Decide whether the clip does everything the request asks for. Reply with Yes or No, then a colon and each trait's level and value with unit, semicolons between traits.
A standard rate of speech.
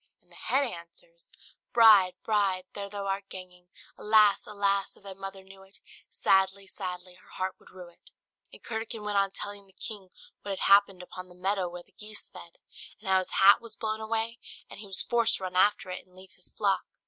No: fast, 215 wpm